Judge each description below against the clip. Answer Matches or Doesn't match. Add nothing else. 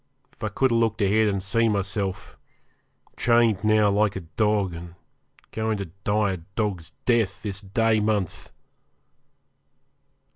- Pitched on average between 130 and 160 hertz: Doesn't match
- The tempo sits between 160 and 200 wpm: Doesn't match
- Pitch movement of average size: Doesn't match